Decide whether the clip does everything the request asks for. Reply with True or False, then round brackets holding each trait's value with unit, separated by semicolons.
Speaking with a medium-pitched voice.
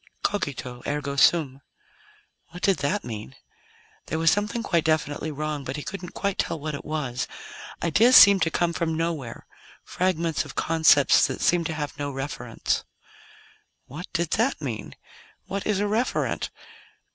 True (160 Hz)